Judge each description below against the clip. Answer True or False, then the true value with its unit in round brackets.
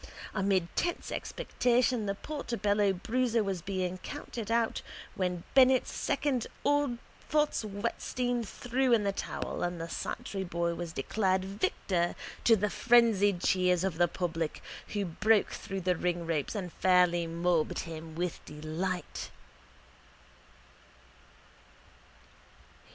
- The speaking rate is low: True (120 wpm)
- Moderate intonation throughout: True (4.7 semitones)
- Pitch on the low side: False (190 Hz)